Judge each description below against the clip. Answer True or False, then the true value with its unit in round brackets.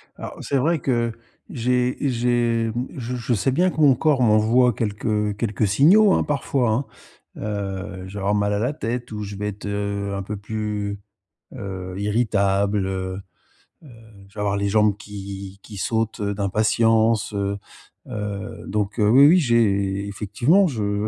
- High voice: False (105 Hz)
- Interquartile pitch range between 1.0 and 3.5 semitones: True (3.1 semitones)